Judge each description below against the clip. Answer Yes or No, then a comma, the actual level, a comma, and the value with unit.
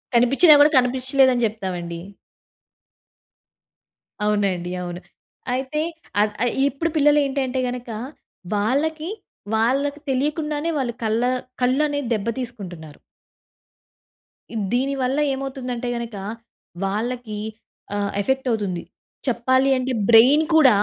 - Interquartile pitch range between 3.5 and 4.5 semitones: Yes, average, 3.9 semitones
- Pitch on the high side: Yes, very high, 250 Hz